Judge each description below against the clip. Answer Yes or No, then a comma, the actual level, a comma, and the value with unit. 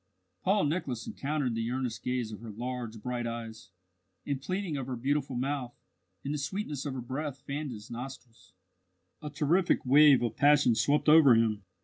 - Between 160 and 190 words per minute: Yes, average, 170 wpm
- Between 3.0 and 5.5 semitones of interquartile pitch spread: Yes, average, 3.8 semitones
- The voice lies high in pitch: No, low, 130 Hz